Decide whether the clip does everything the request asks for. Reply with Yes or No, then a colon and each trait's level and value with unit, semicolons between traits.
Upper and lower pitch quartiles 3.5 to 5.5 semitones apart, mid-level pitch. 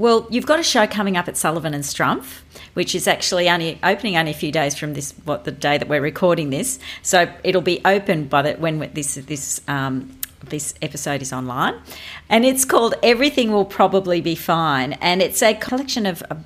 Yes: average, 4.7 semitones; medium, 170 Hz